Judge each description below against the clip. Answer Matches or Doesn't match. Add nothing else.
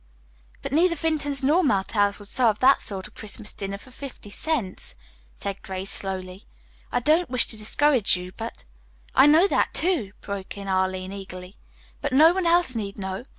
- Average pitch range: Doesn't match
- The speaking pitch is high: Matches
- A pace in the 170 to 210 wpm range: Matches